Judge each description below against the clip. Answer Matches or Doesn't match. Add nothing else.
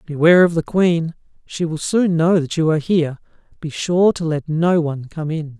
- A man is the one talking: Matches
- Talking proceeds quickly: Matches